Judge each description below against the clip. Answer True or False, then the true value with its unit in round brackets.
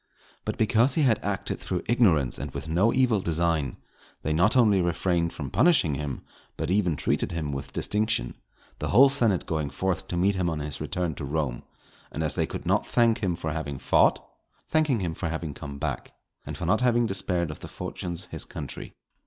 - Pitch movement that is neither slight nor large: False (5.9 semitones)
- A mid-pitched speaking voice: False (85 Hz)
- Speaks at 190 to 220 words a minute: True (200 wpm)